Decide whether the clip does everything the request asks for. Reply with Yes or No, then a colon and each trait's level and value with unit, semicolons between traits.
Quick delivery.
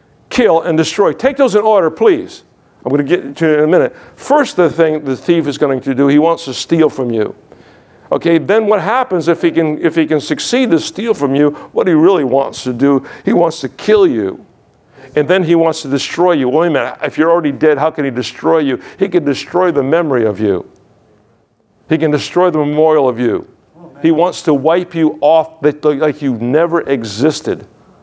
Yes: fast, 215 wpm